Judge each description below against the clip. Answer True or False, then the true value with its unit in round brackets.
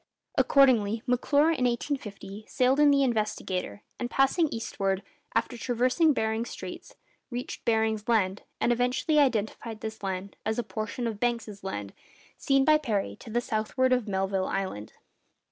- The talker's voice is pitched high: True (230 Hz)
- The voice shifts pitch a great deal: False (3.8 semitones)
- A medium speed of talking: True (145 wpm)